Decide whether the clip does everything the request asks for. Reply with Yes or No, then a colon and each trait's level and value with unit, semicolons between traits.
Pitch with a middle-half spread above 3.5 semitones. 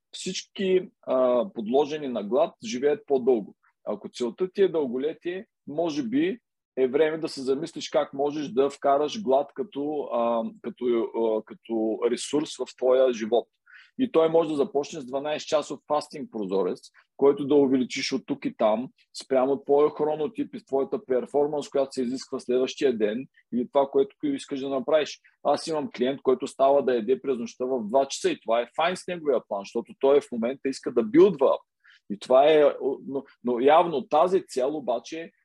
Yes: average, 4.1 semitones